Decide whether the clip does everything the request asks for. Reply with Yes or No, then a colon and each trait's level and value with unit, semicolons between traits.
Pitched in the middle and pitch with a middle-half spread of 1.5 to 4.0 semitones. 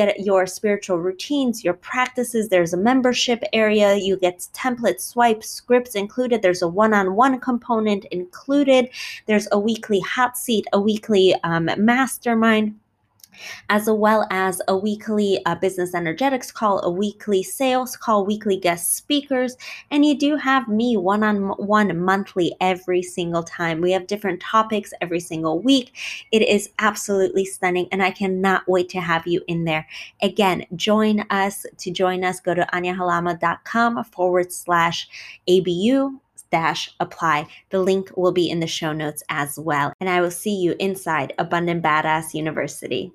No: high, 195 Hz; average, 3.6 semitones